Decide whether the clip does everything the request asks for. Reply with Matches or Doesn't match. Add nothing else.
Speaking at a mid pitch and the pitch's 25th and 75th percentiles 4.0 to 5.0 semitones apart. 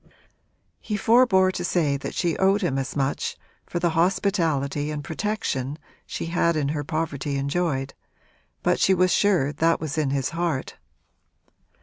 Matches